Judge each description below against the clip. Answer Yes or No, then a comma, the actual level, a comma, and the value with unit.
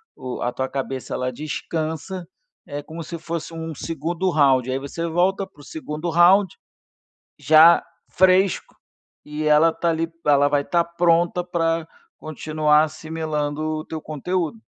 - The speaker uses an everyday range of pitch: No, narrow, 2.3 semitones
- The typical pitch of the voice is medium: Yes, medium, 160 Hz